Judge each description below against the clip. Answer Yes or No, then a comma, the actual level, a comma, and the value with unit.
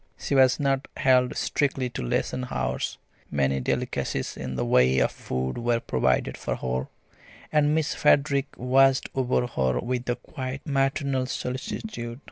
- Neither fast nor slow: Yes, average, 145 wpm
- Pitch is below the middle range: Yes, low, 125 Hz